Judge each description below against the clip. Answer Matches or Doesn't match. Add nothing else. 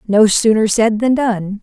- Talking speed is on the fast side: Doesn't match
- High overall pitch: Matches